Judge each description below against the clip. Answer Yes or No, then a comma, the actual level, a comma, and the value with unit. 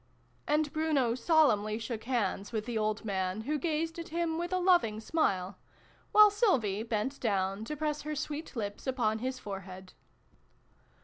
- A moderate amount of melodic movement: No, wide, 6.6 semitones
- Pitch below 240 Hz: No, high, 245 Hz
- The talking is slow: No, average, 165 wpm